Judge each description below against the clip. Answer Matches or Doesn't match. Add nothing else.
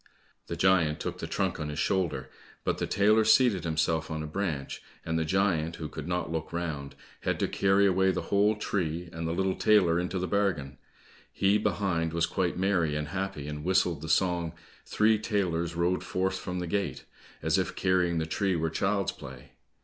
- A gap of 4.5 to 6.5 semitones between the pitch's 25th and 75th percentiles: Doesn't match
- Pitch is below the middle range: Matches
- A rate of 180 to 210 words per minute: Matches